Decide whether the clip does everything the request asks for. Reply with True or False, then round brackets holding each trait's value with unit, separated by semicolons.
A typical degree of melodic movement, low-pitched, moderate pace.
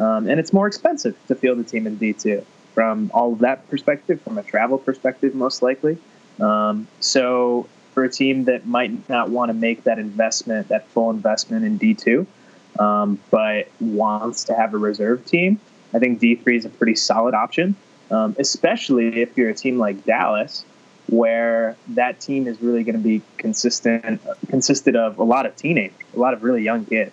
True (3.8 semitones; 120 Hz; 190 wpm)